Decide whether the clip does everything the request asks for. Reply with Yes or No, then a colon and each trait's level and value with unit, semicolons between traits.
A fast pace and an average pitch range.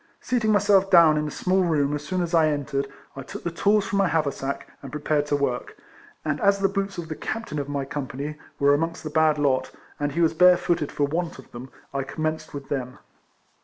Yes: fast, 235 wpm; average, 3.8 semitones